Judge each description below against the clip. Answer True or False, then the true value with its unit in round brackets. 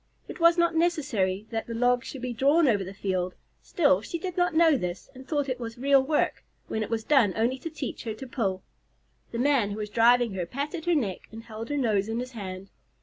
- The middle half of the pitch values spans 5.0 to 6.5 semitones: True (5.4 semitones)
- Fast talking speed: True (235 wpm)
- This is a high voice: True (245 Hz)